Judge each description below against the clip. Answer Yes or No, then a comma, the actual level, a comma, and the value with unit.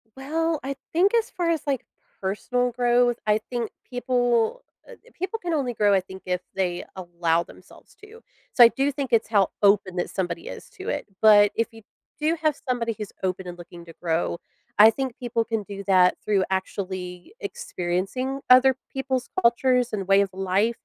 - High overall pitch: Yes, high, 230 Hz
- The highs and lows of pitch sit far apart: Yes, wide, 5.9 semitones